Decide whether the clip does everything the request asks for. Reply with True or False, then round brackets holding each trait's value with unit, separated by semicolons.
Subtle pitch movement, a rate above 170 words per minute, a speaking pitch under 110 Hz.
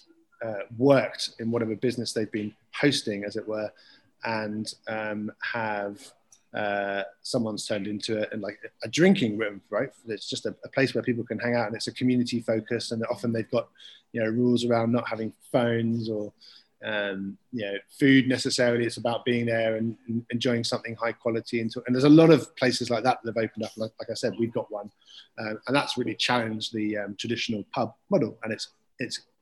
False (2.1 semitones; 200 wpm; 115 Hz)